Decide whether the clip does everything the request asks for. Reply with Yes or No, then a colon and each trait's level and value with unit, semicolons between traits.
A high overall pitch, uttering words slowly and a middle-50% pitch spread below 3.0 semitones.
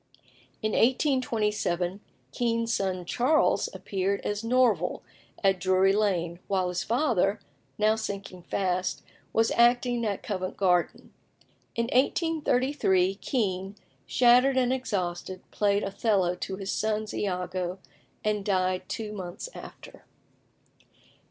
No: high, 205 Hz; slow, 110 wpm; average, 4.1 semitones